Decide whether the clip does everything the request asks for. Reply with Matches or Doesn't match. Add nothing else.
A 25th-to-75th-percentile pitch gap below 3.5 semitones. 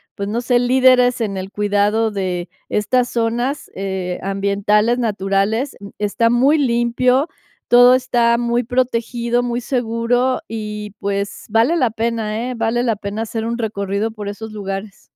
Matches